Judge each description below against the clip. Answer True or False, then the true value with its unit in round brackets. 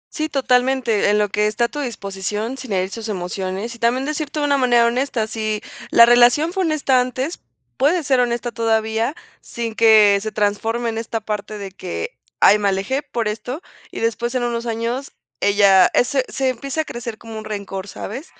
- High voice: True (235 Hz)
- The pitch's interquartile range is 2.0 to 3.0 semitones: False (3.6 semitones)